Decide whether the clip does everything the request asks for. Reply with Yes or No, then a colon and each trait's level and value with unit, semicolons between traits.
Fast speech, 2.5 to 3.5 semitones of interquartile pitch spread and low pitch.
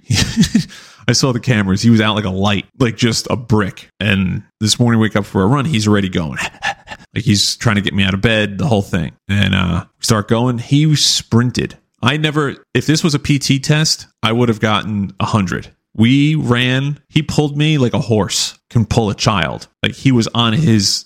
No: fast, 210 wpm; average, 4.7 semitones; low, 115 Hz